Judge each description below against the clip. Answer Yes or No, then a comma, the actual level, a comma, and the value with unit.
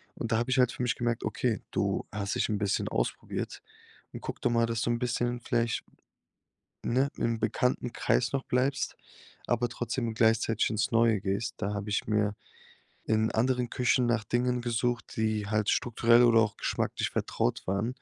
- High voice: No, low, 115 Hz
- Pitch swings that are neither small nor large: No, narrow, 2.0 semitones